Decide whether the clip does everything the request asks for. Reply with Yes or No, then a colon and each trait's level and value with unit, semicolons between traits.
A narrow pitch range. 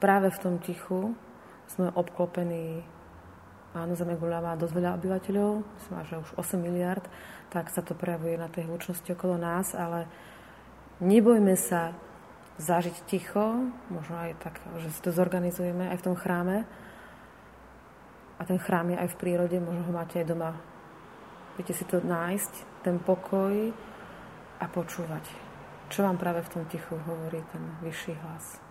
Yes: narrow, 1.6 semitones